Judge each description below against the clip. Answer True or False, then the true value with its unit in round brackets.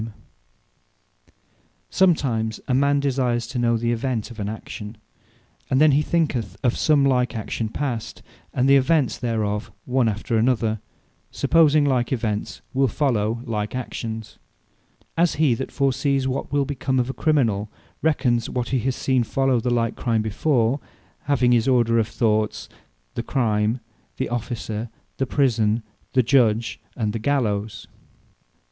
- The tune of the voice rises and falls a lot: False (3.3 semitones)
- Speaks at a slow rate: False (155 wpm)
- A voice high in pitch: False (120 Hz)